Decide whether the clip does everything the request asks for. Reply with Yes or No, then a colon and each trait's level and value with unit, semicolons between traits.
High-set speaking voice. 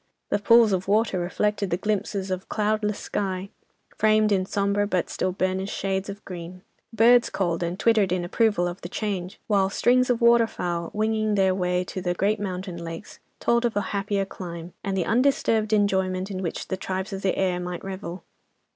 Yes: high, 195 Hz